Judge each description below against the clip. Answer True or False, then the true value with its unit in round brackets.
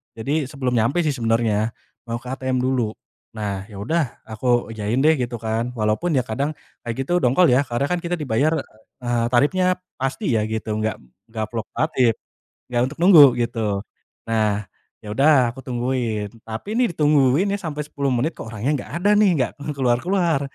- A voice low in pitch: True (125 Hz)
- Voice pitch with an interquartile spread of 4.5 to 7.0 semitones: True (5.0 semitones)